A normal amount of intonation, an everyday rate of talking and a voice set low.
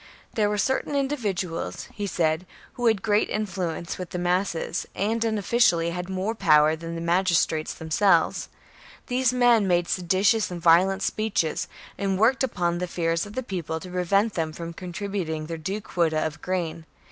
No: average, 3.7 semitones; average, 170 wpm; medium, 185 Hz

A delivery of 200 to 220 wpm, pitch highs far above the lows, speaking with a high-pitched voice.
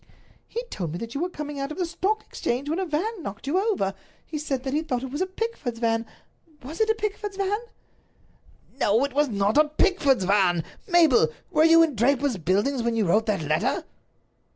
Yes: fast, 205 wpm; wide, 7.5 semitones; very high, 285 Hz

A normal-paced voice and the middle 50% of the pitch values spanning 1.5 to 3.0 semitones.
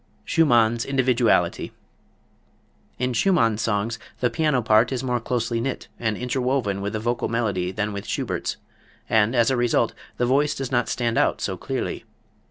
Yes: average, 160 wpm; narrow, 2.4 semitones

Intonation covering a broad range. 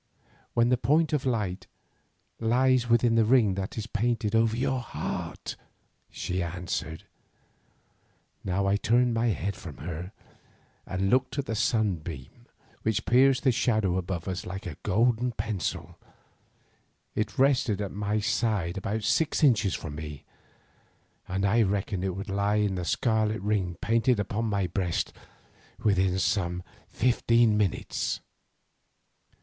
No: average, 3.9 semitones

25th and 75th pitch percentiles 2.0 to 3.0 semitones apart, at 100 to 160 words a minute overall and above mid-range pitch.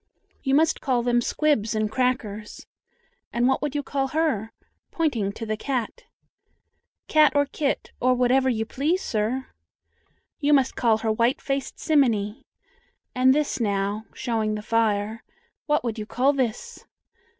No: average, 4.3 semitones; average, 150 wpm; very high, 250 Hz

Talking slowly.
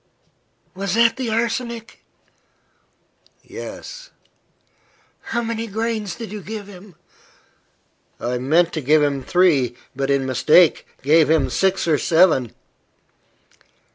Yes: slow, 110 wpm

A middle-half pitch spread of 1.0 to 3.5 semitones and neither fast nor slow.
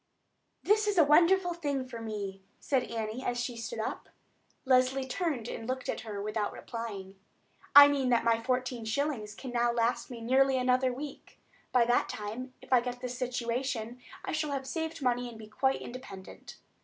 Yes: average, 2.8 semitones; average, 180 wpm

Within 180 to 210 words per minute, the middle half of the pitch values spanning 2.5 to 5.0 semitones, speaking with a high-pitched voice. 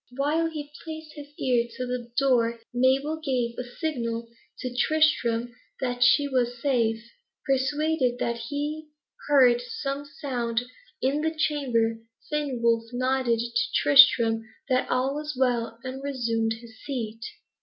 No: slow, 135 wpm; average, 3.5 semitones; very high, 255 Hz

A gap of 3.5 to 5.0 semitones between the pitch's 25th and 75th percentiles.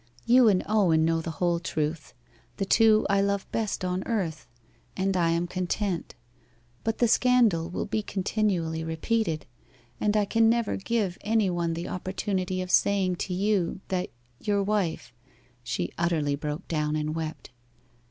Yes: average, 4.1 semitones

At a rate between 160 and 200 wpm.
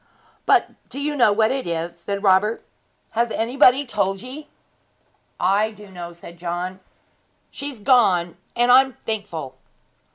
No: average, 140 wpm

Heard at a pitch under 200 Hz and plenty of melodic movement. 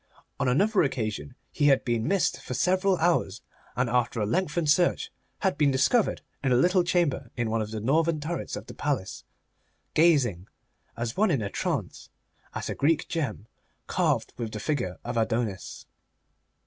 Yes: low, 135 Hz; wide, 6.6 semitones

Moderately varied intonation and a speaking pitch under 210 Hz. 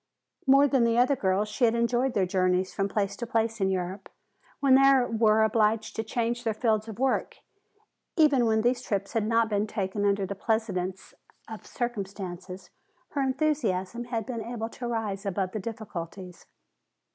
No: average, 3.4 semitones; high, 220 Hz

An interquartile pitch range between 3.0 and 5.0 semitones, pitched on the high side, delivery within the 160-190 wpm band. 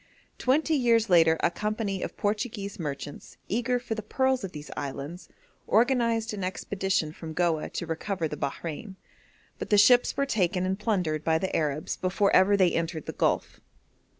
No: wide, 5.4 semitones; high, 195 Hz; average, 170 wpm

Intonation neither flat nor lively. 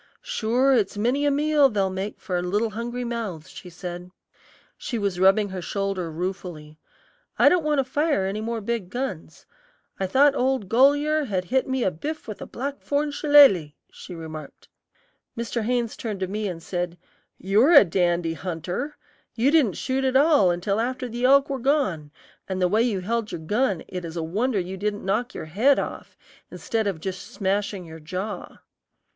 No: wide, 6.2 semitones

